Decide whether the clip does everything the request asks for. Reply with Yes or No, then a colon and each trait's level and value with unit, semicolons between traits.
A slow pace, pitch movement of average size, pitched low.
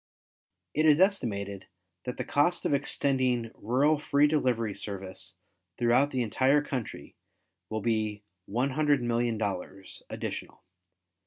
Yes: slow, 105 wpm; average, 5.0 semitones; low, 125 Hz